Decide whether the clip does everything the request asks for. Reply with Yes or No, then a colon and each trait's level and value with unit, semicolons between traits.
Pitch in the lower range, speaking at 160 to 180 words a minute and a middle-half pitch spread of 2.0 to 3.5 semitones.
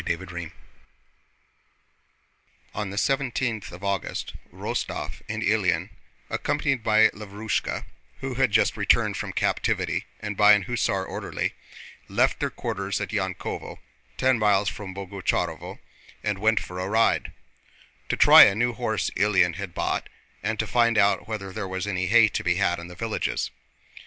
No: low, 105 Hz; average, 150 wpm; average, 2.7 semitones